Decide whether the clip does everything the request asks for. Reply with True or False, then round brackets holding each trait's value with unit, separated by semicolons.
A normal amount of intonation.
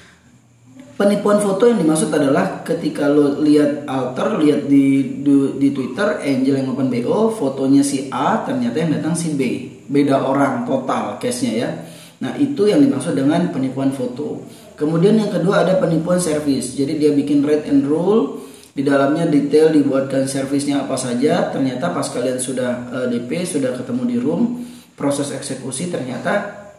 False (6.9 semitones)